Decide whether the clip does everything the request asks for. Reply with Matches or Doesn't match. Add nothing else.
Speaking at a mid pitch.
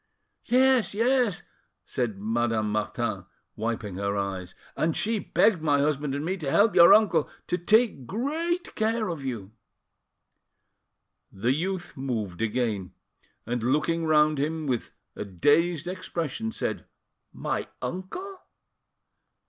Matches